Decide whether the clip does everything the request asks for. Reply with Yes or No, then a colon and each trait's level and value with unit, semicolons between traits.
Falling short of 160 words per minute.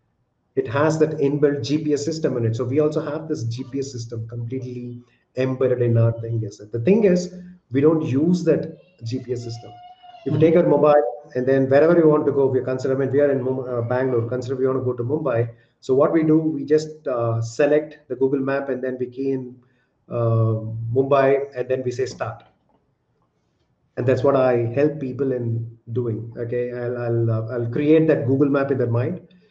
No: average, 200 wpm